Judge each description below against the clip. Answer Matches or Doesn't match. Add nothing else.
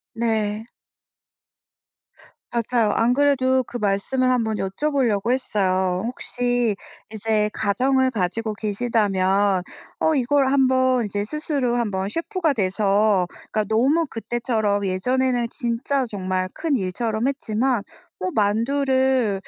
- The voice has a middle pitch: Doesn't match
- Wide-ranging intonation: Doesn't match